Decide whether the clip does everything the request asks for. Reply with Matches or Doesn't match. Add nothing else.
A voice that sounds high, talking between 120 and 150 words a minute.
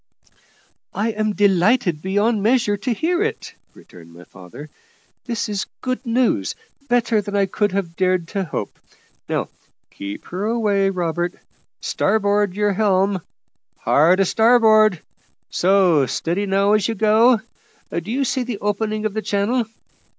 Matches